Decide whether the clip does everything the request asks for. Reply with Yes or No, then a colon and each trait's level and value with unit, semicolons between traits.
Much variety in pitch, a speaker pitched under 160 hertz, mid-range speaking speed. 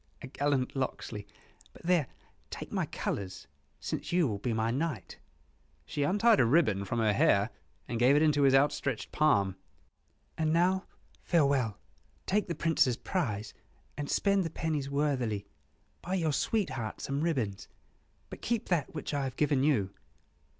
Yes: wide, 6.1 semitones; medium, 140 Hz; average, 155 wpm